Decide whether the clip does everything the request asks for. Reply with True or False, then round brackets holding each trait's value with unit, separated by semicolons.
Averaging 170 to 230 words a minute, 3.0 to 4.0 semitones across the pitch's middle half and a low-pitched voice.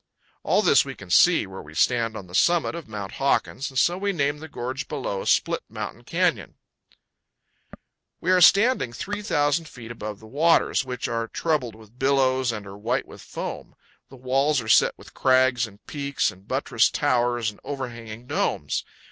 False (175 wpm; 4.6 semitones; 125 Hz)